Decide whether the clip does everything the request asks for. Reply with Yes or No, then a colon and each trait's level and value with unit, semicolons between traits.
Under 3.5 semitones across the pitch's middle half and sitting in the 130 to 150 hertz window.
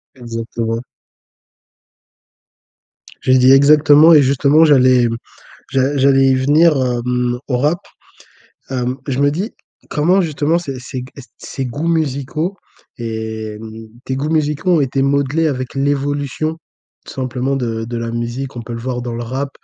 Yes: average, 3.1 semitones; low, 135 Hz